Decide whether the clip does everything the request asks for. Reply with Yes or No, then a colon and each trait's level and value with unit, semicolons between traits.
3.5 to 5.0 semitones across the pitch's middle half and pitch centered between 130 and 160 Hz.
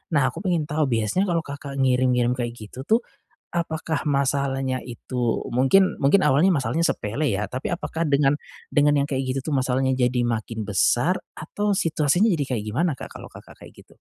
Yes: average, 4.2 semitones; medium, 140 Hz